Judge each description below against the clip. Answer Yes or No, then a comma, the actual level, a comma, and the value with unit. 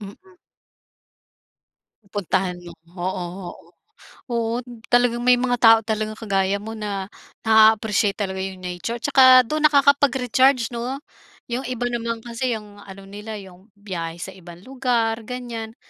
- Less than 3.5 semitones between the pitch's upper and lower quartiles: No, average, 3.8 semitones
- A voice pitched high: Yes, high, 220 Hz